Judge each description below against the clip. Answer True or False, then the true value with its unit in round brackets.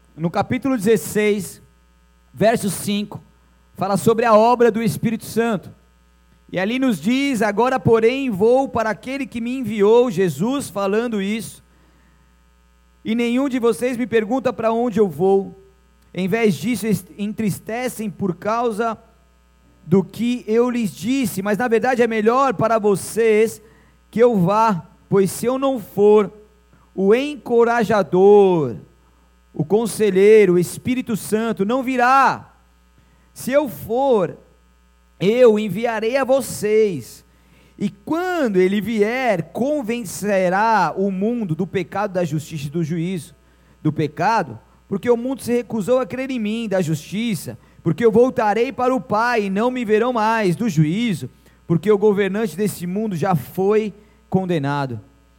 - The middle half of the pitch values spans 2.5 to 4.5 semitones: False (5.2 semitones)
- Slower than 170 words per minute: True (140 wpm)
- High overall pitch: True (210 Hz)